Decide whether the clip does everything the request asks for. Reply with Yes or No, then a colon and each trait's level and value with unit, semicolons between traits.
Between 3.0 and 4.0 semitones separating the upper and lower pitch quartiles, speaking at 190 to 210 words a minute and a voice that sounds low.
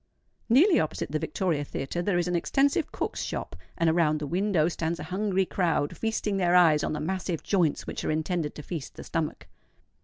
No: average, 3.6 semitones; average, 195 wpm; medium, 175 Hz